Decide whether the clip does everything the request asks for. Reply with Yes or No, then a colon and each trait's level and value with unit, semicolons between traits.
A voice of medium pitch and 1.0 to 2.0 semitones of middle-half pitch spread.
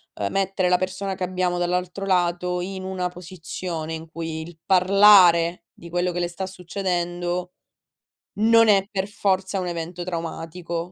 Yes: medium, 180 Hz; narrow, 1.6 semitones